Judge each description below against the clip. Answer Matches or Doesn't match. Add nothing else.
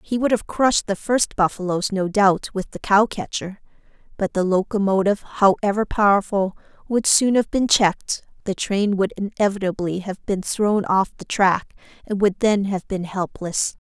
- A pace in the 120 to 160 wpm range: Doesn't match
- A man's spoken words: Doesn't match